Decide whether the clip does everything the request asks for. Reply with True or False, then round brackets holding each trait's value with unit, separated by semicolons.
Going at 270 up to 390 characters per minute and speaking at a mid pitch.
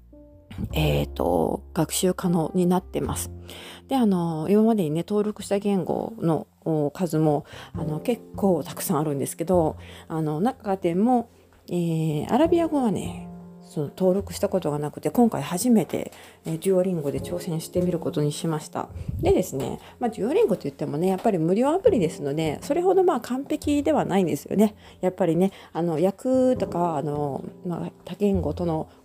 True (335 characters per minute; 180 Hz)